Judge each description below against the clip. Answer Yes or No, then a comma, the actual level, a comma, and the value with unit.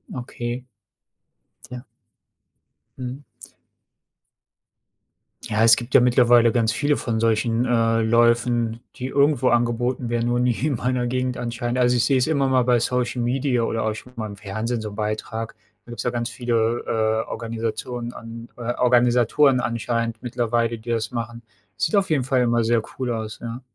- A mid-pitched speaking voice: No, low, 120 Hz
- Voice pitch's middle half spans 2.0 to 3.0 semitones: No, narrow, 1.5 semitones